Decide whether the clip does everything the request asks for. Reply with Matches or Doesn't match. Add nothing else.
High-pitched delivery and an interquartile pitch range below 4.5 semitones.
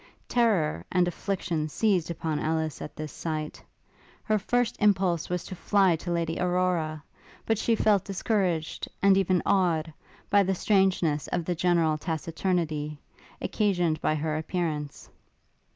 Doesn't match